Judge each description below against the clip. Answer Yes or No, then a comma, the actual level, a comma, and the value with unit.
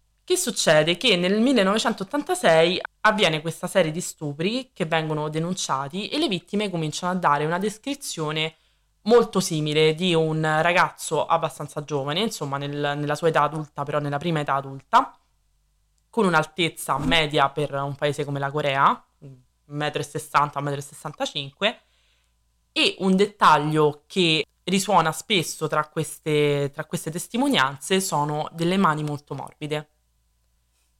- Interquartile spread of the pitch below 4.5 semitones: Yes, average, 4.0 semitones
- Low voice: No, medium, 155 Hz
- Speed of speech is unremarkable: Yes, average, 130 wpm